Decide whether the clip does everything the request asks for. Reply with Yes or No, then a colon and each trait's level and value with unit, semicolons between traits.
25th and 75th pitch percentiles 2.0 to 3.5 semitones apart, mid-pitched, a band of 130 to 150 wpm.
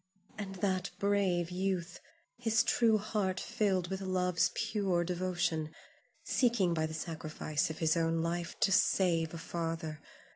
Yes: average, 2.9 semitones; medium, 180 Hz; average, 140 wpm